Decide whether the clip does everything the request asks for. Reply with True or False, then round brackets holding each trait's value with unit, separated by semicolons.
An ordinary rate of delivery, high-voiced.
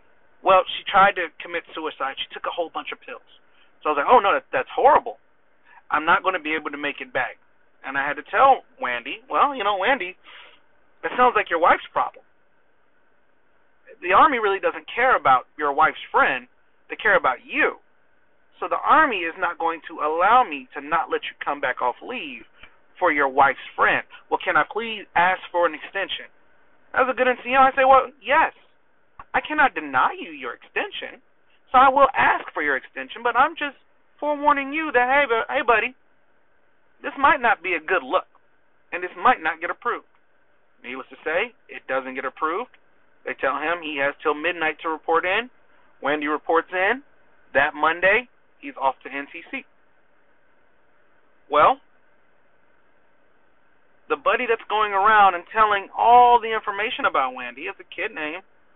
True (180 wpm; 240 Hz)